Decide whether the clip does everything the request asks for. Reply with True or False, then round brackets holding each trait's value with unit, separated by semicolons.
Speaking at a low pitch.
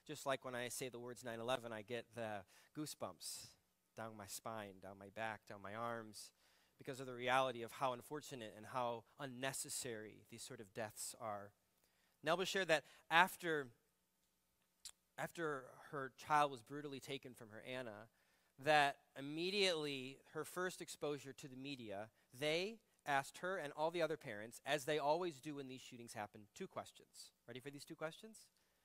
True (130 Hz)